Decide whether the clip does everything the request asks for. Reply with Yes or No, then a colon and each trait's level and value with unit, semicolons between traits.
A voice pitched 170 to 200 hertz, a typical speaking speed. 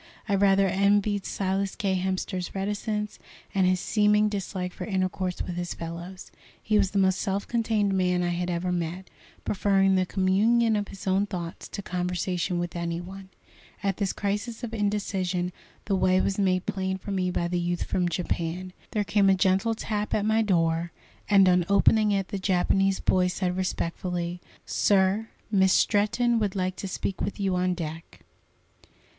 Yes: high, 190 Hz; average, 175 wpm